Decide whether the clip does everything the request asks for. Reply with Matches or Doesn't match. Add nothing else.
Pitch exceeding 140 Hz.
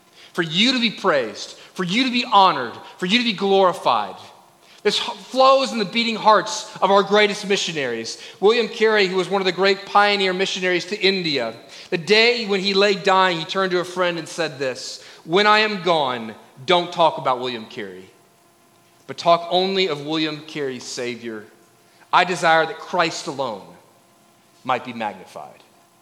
Matches